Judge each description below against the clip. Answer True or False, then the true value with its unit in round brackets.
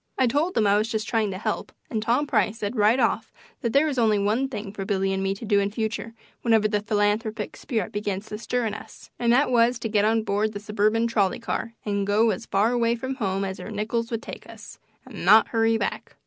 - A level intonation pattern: True (2.1 semitones)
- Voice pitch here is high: True (220 Hz)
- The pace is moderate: False (245 wpm)